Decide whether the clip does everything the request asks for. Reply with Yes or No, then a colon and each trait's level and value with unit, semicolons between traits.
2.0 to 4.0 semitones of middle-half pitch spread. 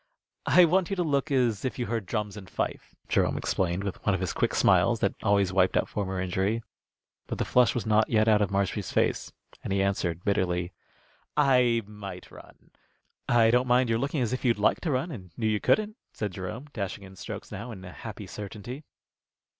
No: average, 4.4 semitones